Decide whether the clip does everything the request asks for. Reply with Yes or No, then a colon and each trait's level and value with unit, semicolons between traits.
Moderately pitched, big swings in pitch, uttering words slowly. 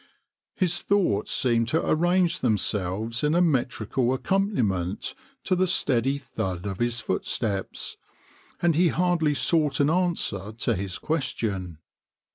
No: low, 130 Hz; wide, 8.3 semitones; slow, 130 wpm